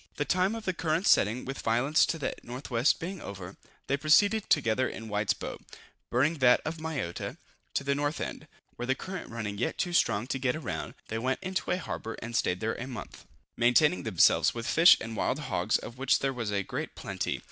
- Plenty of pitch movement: Yes, wide, 5.9 semitones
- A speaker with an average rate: No, fast, 210 wpm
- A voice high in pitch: No, low, 130 Hz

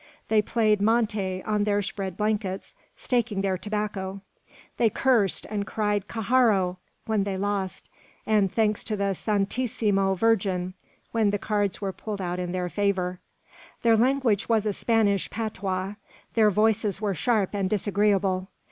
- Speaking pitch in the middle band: No, high, 205 Hz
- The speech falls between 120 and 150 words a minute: Yes, average, 145 wpm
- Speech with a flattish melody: Yes, narrow, 2.1 semitones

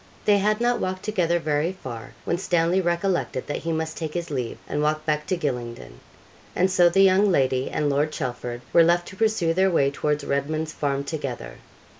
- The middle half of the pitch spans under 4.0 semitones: No, average, 4.7 semitones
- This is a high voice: No, medium, 160 Hz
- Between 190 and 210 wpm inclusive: Yes, average, 195 wpm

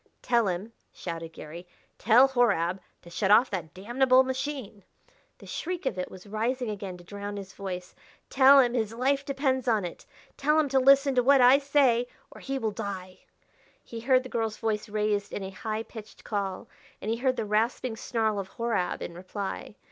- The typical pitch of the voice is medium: No, high, 225 Hz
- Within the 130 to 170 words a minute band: No, average, 195 wpm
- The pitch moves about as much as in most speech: Yes, average, 4.7 semitones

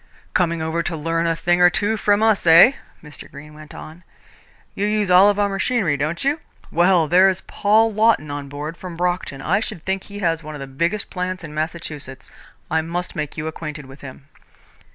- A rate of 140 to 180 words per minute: No, average, 195 wpm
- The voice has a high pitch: No, medium, 170 Hz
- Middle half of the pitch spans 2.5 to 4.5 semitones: Yes, average, 4.1 semitones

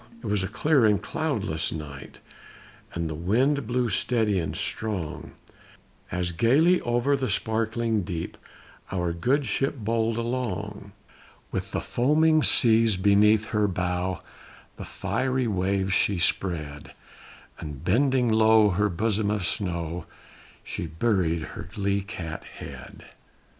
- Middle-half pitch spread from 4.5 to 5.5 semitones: Yes, average, 4.9 semitones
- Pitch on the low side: Yes, low, 105 Hz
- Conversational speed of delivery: No, slow, 125 wpm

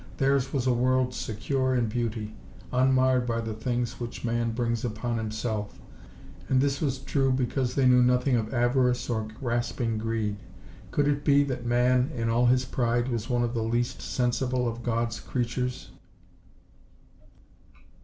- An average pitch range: No, narrow, 1.8 semitones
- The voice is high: No, low, 120 Hz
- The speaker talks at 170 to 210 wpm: No, average, 155 wpm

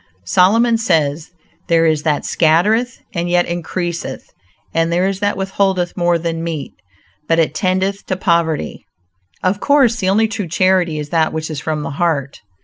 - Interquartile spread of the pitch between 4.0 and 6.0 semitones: No, average, 3.1 semitones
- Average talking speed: Yes, average, 165 wpm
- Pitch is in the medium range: Yes, medium, 175 Hz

